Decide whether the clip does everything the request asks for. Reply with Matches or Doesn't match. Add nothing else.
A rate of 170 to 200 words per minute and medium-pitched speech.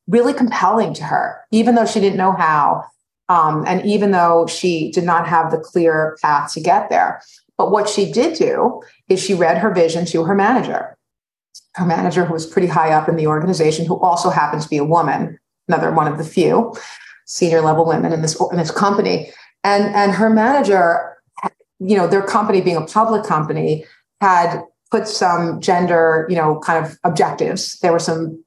Matches